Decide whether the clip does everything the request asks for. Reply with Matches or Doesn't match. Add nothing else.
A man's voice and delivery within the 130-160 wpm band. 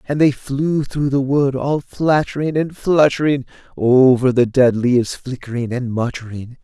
Matches